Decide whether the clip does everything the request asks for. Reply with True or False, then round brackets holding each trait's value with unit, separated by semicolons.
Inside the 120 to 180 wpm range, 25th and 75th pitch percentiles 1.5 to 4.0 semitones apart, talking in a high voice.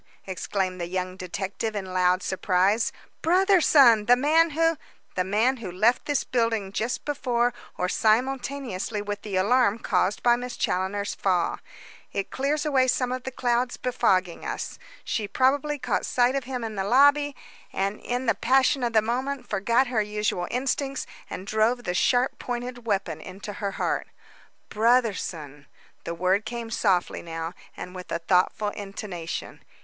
False (160 wpm; 5.0 semitones; 225 Hz)